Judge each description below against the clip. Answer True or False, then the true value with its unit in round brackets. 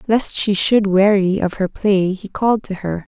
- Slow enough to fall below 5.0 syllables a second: True (4.5 syllables/s)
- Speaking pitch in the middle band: False (200 Hz)